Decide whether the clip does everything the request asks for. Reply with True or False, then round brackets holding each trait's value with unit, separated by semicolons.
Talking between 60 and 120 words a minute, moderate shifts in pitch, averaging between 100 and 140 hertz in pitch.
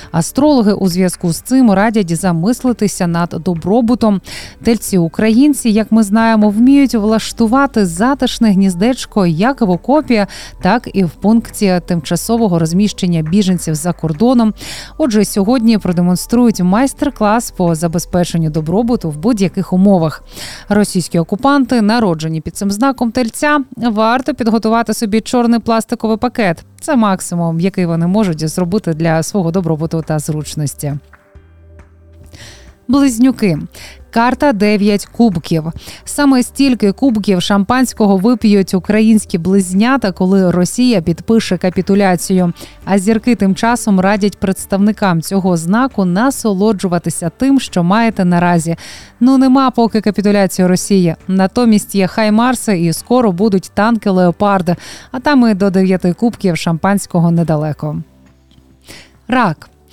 False (115 wpm; 4.8 semitones; 200 Hz)